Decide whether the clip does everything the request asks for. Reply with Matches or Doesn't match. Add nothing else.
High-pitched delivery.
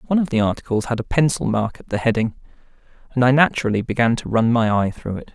Doesn't match